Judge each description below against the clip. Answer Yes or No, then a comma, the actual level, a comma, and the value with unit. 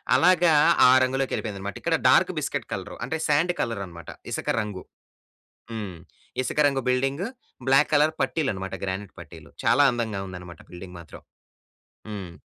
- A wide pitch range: Yes, wide, 6.7 semitones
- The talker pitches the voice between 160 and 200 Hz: No, low, 110 Hz